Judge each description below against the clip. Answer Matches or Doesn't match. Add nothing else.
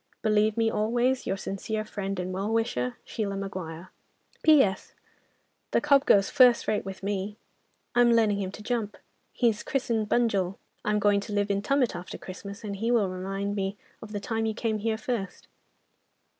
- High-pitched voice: Matches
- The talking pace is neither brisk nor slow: Matches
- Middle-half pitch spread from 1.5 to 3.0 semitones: Matches